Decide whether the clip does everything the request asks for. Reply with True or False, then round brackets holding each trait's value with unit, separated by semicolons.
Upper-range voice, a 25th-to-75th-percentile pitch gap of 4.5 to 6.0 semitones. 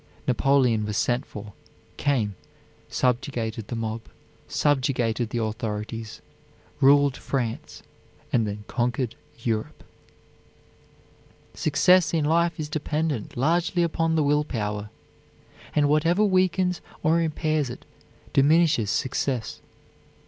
False (135 Hz; 5.5 semitones)